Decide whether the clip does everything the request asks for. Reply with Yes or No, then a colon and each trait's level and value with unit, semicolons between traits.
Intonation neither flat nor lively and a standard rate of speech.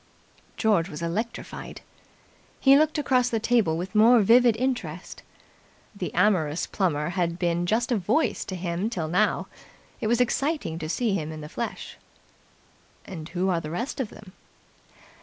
No: wide, 5.9 semitones; average, 160 wpm